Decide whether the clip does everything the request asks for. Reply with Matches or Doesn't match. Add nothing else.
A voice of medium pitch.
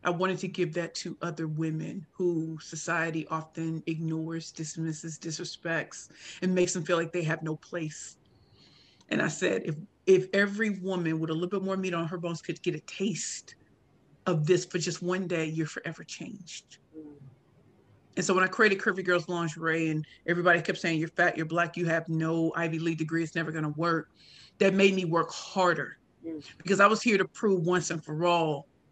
Matches